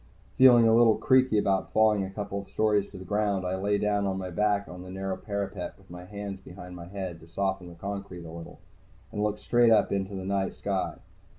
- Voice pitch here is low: Yes, low, 100 Hz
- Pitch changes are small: Yes, narrow, 1.9 semitones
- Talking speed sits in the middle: No, fast, 220 wpm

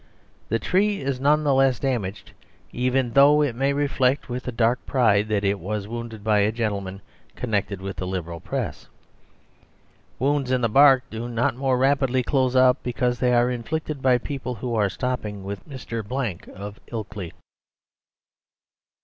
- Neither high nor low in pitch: No, low, 125 Hz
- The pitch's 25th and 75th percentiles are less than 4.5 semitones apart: Yes, average, 4.1 semitones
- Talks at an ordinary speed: Yes, average, 165 wpm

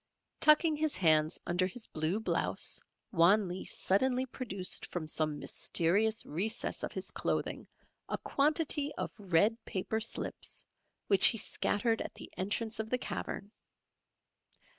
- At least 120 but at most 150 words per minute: Yes, average, 140 wpm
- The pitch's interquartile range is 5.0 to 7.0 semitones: Yes, wide, 5.4 semitones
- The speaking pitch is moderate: No, high, 205 Hz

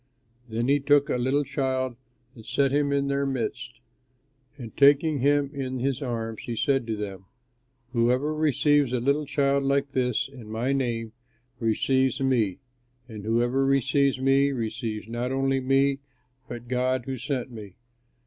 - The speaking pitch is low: Yes, low, 130 Hz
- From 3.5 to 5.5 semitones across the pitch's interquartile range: No, average, 2.7 semitones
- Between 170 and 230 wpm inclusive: No, average, 155 wpm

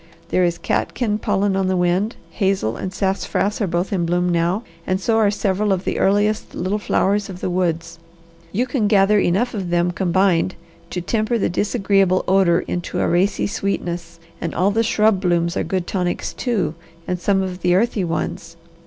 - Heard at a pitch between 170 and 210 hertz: Yes, high, 190 Hz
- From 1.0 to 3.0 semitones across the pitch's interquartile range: Yes, average, 2.7 semitones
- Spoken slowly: No, average, 185 wpm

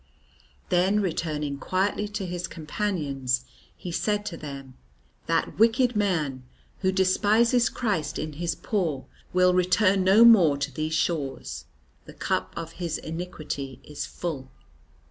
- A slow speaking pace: Yes, slow, 130 wpm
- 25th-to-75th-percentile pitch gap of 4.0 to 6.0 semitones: Yes, average, 5.1 semitones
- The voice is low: No, medium, 175 Hz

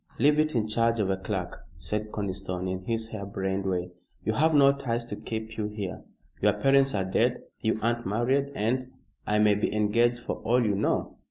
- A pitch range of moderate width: Yes, average, 3.2 semitones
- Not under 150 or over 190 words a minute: No, fast, 205 wpm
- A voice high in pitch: No, low, 110 Hz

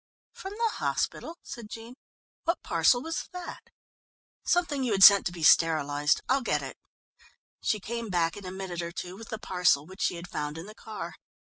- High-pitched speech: Yes, high, 200 Hz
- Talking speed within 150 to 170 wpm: No, average, 190 wpm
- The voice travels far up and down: Yes, wide, 6.2 semitones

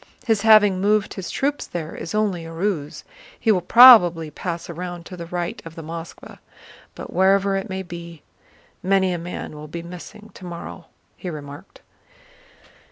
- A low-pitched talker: No, medium, 175 Hz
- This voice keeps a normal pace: Yes, average, 165 wpm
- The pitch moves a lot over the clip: No, average, 2.9 semitones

